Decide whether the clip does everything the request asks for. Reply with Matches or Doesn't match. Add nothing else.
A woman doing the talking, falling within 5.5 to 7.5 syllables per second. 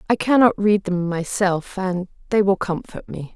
Doesn't match